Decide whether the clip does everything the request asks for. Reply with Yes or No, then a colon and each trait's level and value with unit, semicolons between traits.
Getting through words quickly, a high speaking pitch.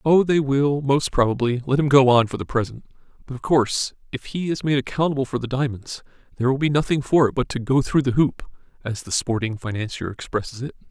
No: fast, 225 wpm; low, 130 Hz